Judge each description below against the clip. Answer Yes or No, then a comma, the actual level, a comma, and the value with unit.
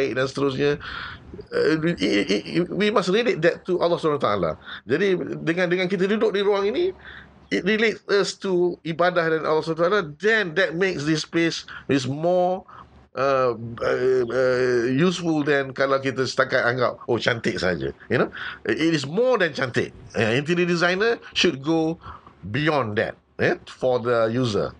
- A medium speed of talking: No, fast, 160 wpm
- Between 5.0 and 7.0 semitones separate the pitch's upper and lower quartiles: Yes, wide, 5.6 semitones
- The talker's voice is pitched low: No, medium, 165 Hz